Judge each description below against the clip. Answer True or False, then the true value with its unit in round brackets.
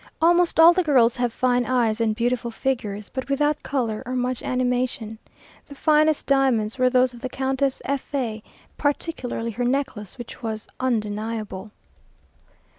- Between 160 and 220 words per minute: False (150 wpm)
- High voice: True (250 Hz)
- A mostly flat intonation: False (3.0 semitones)